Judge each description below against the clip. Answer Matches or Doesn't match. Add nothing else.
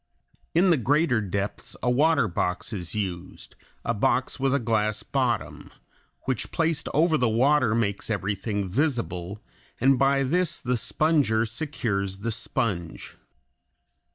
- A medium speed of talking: Doesn't match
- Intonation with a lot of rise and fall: Matches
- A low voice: Matches